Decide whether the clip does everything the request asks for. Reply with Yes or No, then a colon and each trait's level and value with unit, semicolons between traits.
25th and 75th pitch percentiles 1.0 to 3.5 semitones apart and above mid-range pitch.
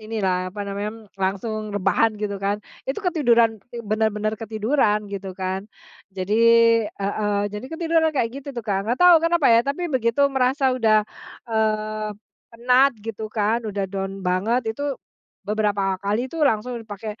Yes: average, 2.9 semitones; high, 215 Hz